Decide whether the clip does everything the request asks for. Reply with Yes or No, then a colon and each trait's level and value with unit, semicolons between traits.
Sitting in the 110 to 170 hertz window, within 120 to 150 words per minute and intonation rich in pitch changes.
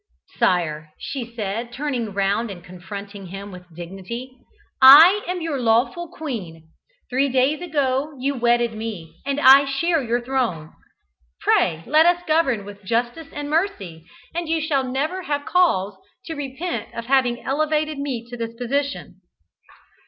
No: very high, 255 Hz; average, 145 wpm; wide, 6.4 semitones